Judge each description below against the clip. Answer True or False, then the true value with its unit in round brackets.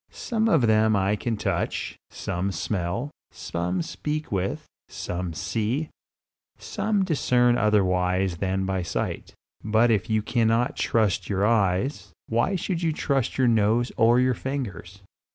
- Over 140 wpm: False (135 wpm)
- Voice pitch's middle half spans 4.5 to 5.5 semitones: True (4.9 semitones)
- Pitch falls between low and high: False (110 Hz)